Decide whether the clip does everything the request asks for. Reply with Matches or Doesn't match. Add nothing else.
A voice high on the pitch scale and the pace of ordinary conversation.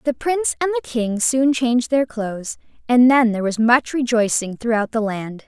Matches